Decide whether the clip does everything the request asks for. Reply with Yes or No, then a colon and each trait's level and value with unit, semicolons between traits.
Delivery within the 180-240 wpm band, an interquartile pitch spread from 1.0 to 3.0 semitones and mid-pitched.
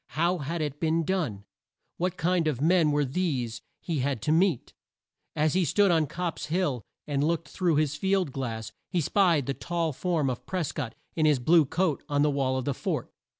No: average, 200 wpm; average, 3.9 semitones; medium, 155 Hz